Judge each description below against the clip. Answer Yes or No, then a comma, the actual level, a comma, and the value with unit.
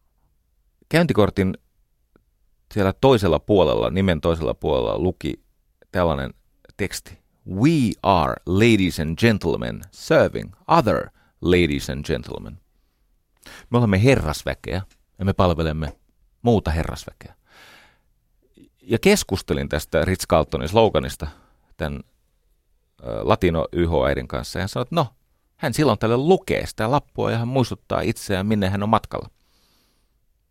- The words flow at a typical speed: Yes, average, 110 wpm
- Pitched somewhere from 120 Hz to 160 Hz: No, very low, 90 Hz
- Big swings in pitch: Yes, wide, 6.2 semitones